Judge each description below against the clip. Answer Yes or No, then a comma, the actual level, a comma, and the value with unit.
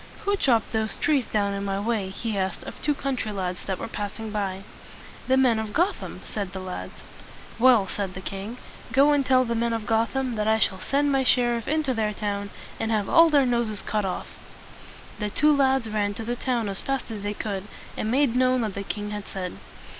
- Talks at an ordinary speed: No, fast, 220 wpm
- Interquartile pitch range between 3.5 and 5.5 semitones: Yes, average, 4.1 semitones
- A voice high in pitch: Yes, high, 220 Hz